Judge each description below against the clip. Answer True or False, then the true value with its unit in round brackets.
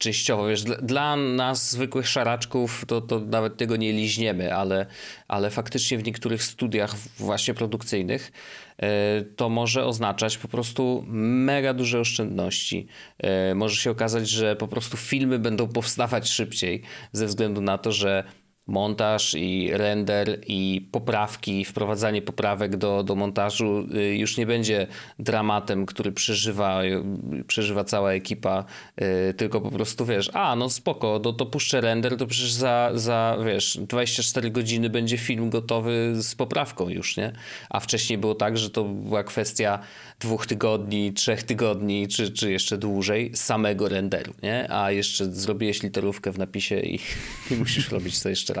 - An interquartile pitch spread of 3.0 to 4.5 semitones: False (2.6 semitones)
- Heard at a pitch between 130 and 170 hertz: False (110 Hz)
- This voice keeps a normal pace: True (145 wpm)